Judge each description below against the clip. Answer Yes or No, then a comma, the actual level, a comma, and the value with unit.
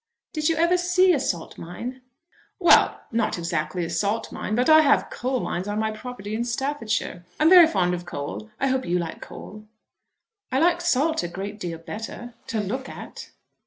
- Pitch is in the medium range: No, high, 225 Hz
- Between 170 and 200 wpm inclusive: Yes, average, 190 wpm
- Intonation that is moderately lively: No, wide, 7.9 semitones